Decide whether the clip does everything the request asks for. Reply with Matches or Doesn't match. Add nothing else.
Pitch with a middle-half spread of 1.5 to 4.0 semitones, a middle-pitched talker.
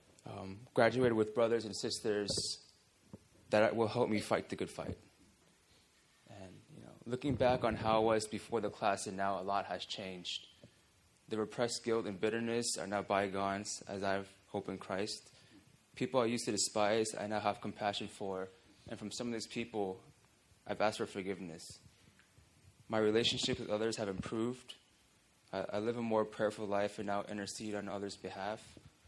Doesn't match